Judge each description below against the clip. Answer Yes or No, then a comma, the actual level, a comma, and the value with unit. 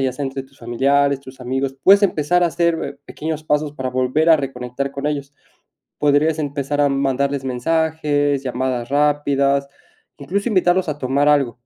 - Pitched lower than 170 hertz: Yes, medium, 140 Hz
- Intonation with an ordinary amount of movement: No, narrow, 2.1 semitones